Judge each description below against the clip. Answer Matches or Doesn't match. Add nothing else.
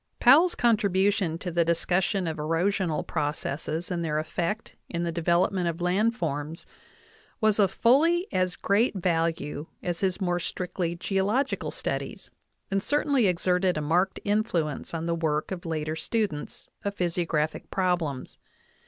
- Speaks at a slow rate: Doesn't match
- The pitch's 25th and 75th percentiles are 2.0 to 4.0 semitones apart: Matches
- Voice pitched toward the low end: Doesn't match